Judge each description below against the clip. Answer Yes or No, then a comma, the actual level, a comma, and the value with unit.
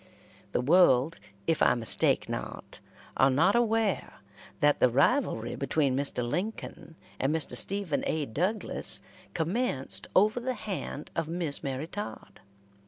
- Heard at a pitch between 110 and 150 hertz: No, medium, 160 Hz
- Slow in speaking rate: Yes, slow, 130 wpm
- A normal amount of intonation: No, wide, 6.8 semitones